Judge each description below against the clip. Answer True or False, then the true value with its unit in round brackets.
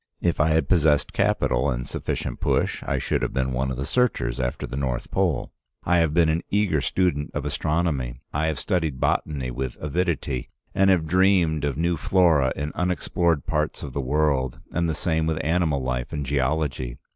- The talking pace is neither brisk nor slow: True (190 wpm)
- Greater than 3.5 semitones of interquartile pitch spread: True (4.3 semitones)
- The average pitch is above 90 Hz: False (75 Hz)